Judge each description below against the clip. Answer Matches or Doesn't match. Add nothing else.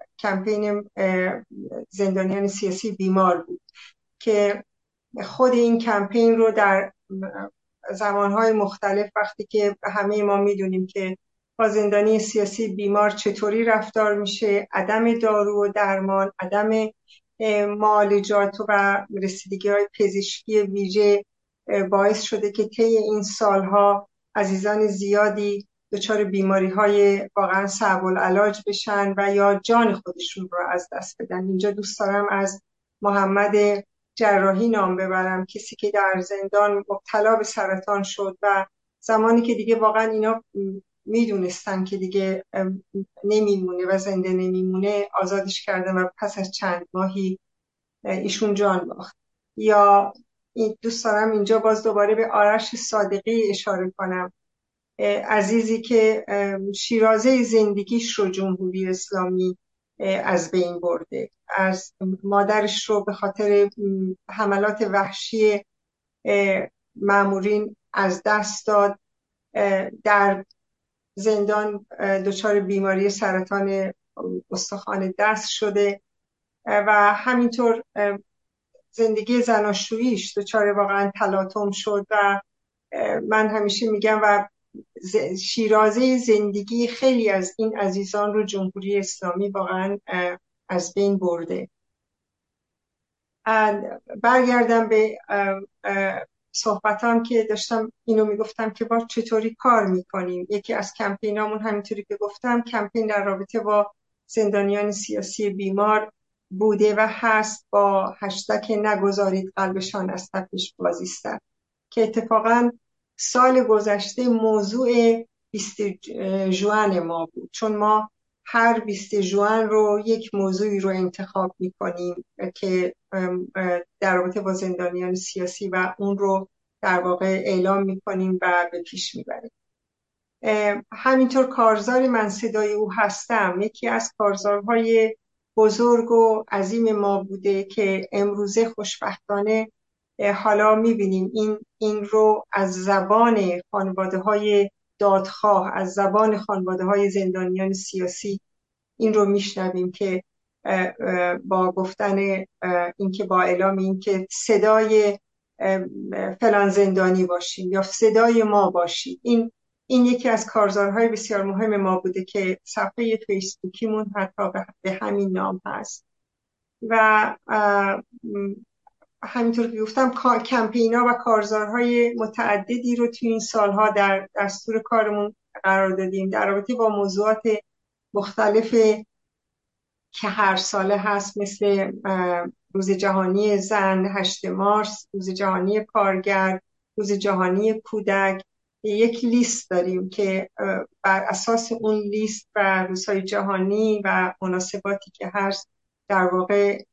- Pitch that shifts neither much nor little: Doesn't match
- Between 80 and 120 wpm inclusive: Matches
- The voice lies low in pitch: Doesn't match